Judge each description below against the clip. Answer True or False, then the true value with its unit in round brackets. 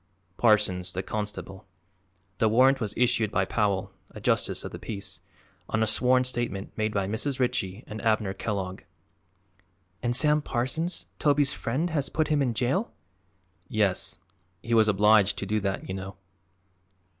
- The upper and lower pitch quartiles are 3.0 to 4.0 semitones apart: False (4.4 semitones)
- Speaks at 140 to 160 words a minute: True (155 wpm)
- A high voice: False (110 Hz)